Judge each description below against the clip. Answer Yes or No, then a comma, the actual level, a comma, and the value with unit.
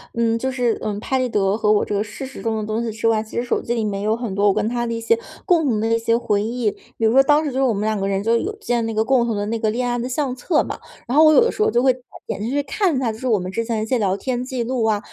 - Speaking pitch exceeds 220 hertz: Yes, high, 230 Hz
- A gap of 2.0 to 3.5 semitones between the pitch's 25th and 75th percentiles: Yes, average, 3.0 semitones